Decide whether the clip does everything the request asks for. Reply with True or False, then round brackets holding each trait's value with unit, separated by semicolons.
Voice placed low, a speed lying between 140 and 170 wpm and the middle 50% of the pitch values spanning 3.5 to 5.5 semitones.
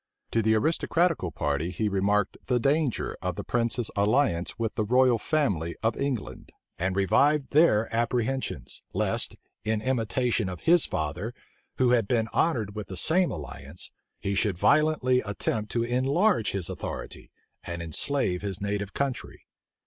True (110 Hz; 150 wpm; 5.1 semitones)